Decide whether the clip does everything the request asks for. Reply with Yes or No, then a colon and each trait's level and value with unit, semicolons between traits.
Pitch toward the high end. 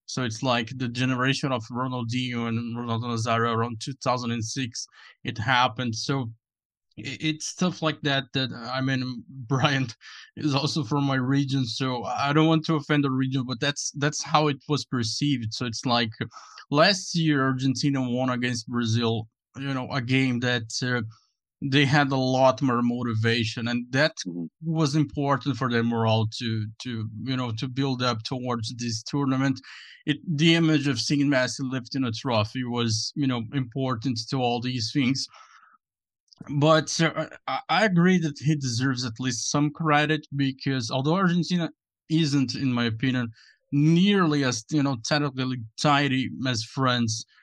No: low, 130 Hz